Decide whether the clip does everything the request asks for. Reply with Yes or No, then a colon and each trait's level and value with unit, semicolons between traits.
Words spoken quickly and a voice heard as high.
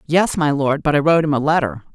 No: fast, 275 wpm; medium, 150 Hz